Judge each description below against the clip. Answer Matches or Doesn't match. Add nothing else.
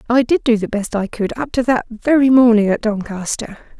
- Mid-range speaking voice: Doesn't match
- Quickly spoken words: Matches